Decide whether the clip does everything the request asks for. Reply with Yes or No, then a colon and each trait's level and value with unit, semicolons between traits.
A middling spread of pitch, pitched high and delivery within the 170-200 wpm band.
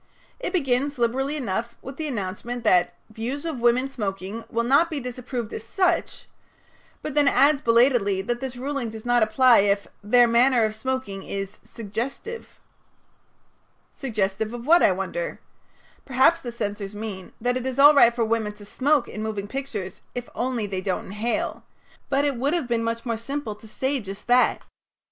Yes: average, 3.9 semitones; high, 240 Hz; average, 180 wpm